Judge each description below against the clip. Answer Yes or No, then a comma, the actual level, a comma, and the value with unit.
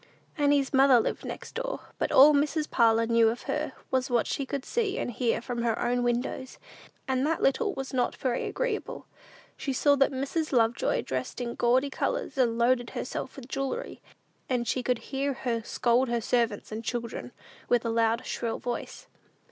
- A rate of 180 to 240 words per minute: Yes, average, 185 wpm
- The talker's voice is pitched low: No, very high, 255 Hz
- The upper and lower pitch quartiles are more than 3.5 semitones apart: No, average, 2.7 semitones